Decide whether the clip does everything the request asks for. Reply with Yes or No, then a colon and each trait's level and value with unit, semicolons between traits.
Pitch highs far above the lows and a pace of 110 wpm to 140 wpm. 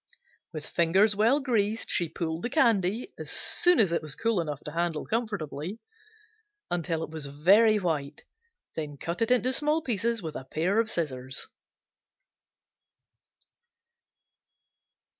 Yes: wide, 6.3 semitones; slow, 135 wpm